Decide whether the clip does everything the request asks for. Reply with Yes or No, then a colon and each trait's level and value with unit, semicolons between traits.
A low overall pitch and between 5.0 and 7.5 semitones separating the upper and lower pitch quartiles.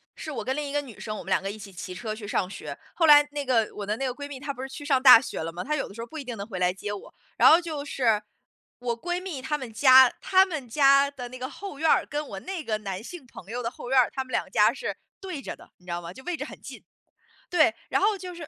No: very high, 260 Hz; wide, 5.6 semitones